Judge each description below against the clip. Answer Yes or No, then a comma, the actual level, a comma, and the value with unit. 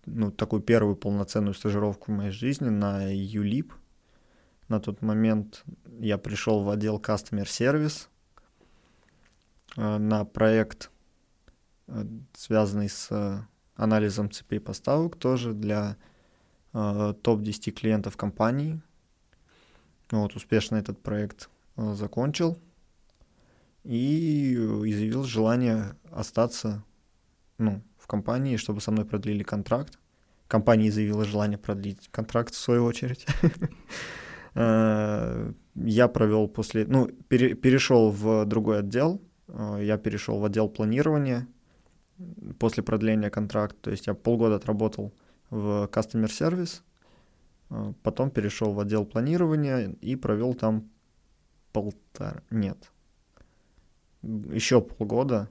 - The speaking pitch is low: Yes, low, 110 Hz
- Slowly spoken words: Yes, slow, 100 wpm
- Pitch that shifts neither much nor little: No, narrow, 2.2 semitones